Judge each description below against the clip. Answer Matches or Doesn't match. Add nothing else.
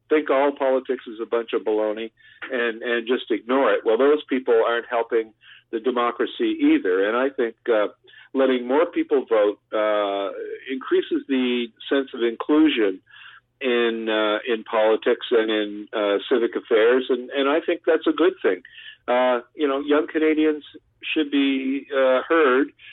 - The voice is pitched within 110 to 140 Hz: Matches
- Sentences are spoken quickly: Doesn't match